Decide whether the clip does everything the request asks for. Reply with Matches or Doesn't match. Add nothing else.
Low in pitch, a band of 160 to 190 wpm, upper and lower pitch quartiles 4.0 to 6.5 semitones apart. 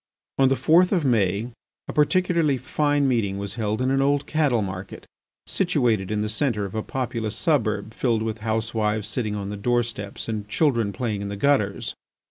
Matches